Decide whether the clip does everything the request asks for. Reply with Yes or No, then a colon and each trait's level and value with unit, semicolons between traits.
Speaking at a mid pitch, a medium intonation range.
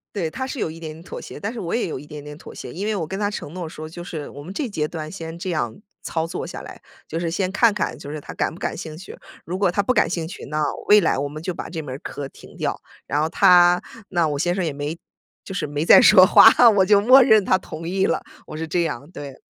Yes: medium, 170 Hz; average, 4.1 semitones